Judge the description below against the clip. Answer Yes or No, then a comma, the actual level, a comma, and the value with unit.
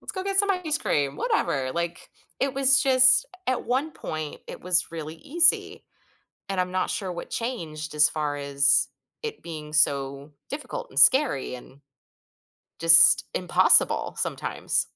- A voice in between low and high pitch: Yes, medium, 170 Hz